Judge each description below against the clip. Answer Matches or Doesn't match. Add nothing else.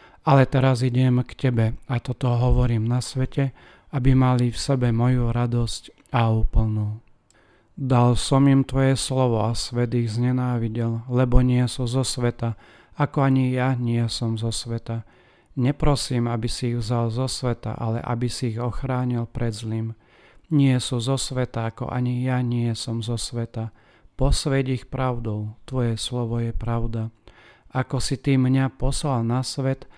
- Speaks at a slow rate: Doesn't match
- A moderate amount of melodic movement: Doesn't match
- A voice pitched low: Matches